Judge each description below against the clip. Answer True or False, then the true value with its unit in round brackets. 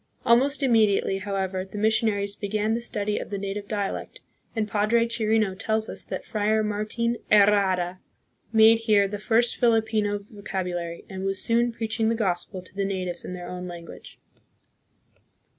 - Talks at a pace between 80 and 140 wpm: False (160 wpm)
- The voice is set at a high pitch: True (210 Hz)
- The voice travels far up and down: False (2.4 semitones)